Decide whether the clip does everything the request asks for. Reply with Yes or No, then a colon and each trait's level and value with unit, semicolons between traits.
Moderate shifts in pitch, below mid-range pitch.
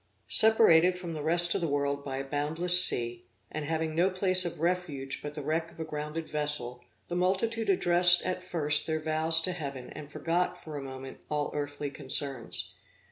No: average, 3.4 semitones; medium, 155 Hz